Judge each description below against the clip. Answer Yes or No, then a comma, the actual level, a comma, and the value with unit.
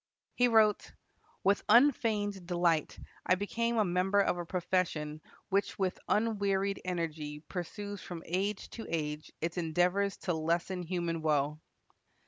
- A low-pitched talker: No, medium, 180 Hz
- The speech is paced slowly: Yes, slow, 130 wpm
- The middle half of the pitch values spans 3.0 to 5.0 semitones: Yes, average, 3.4 semitones